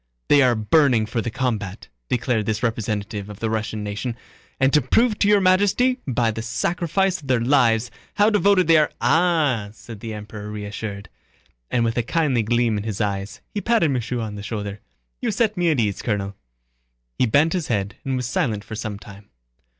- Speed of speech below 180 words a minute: No, average, 195 wpm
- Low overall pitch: Yes, low, 115 Hz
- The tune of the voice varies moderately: No, wide, 6.1 semitones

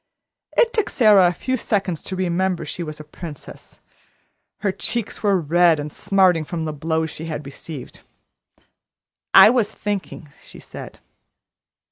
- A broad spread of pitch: No, average, 4.2 semitones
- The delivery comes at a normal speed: Yes, average, 145 wpm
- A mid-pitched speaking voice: Yes, medium, 175 Hz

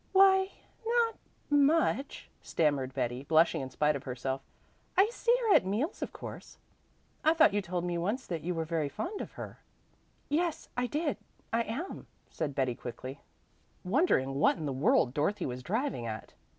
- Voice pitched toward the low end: No, medium, 175 Hz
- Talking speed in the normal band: Yes, average, 175 wpm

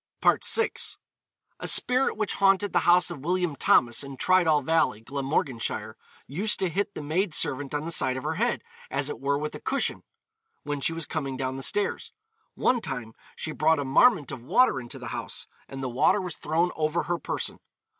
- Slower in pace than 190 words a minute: No, average, 195 wpm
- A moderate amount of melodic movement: Yes, average, 5.0 semitones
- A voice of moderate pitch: Yes, medium, 155 Hz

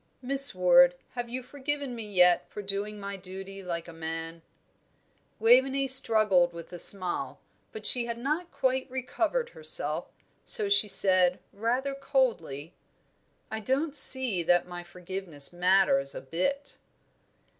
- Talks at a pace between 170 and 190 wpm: No, slow, 135 wpm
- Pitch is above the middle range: Yes, high, 205 Hz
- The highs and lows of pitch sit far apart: Yes, wide, 6.8 semitones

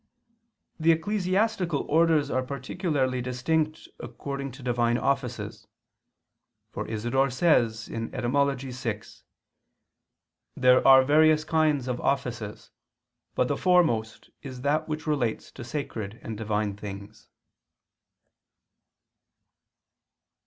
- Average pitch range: Yes, average, 4.4 semitones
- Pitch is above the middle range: No, low, 130 Hz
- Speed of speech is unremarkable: No, slow, 95 wpm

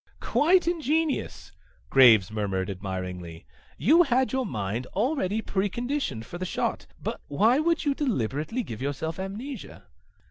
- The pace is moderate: No, slow, 130 wpm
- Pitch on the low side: No, high, 190 Hz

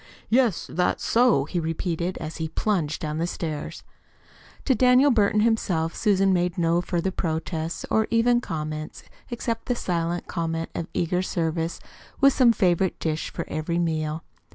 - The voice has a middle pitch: Yes, medium, 175 Hz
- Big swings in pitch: No, average, 4.8 semitones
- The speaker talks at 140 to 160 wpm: Yes, average, 155 wpm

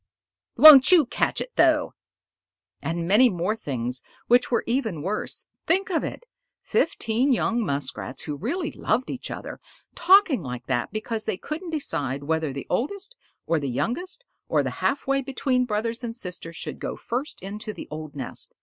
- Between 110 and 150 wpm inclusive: No, average, 170 wpm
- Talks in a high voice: Yes, high, 225 Hz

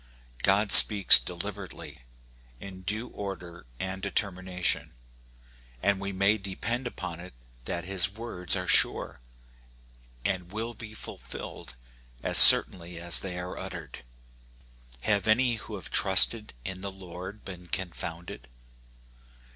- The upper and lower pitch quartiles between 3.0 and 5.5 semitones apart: No, narrow, 2.5 semitones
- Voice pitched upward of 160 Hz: No, very low, 95 Hz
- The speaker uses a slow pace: Yes, slow, 120 wpm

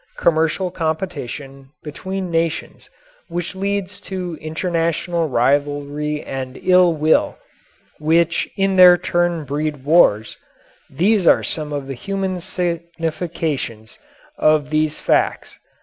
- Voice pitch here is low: No, medium, 165 Hz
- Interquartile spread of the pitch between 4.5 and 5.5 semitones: No, average, 3.3 semitones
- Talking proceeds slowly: Yes, slow, 105 wpm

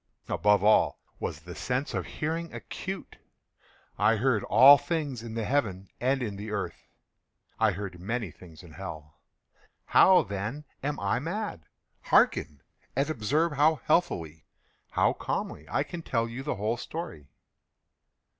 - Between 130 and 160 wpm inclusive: Yes, average, 140 wpm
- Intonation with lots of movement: Yes, wide, 6.9 semitones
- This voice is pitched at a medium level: No, low, 115 Hz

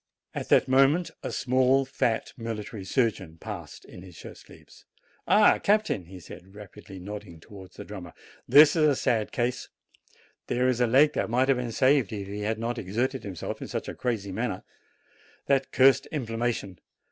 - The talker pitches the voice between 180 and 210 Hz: No, low, 115 Hz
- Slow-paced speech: No, average, 175 wpm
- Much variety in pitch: No, average, 4.8 semitones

